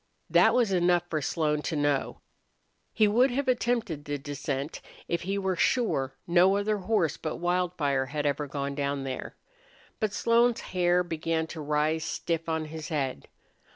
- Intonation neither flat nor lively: Yes, average, 4.8 semitones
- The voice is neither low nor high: Yes, medium, 165 Hz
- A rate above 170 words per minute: No, average, 160 wpm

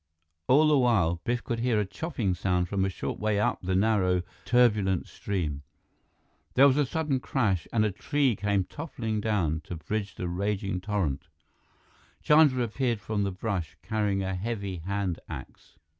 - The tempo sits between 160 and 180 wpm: Yes, average, 165 wpm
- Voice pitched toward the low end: Yes, low, 105 Hz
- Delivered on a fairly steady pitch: No, average, 4.2 semitones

